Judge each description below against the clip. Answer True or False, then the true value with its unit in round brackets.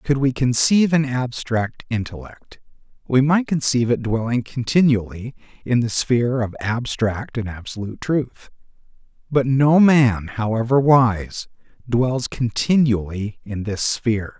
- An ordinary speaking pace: False (125 wpm)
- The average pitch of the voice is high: False (120 Hz)